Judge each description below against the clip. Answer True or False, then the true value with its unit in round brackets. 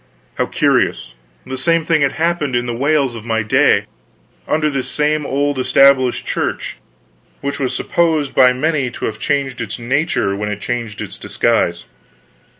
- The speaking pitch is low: True (130 Hz)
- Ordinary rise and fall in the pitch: True (4.2 semitones)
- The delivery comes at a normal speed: True (160 wpm)